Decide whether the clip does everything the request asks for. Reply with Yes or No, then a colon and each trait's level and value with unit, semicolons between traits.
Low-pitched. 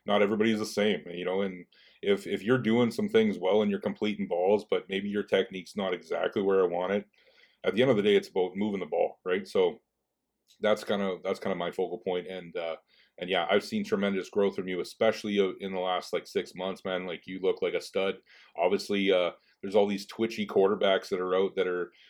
Yes: low, 100 Hz